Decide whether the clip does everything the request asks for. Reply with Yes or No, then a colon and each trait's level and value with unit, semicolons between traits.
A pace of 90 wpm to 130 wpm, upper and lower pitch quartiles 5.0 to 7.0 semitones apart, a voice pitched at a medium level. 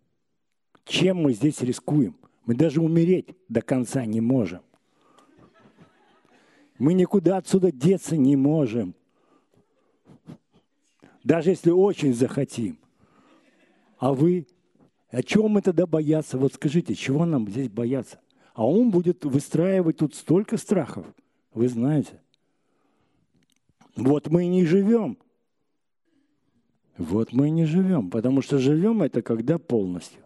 Yes: average, 115 wpm; wide, 5.6 semitones; medium, 150 Hz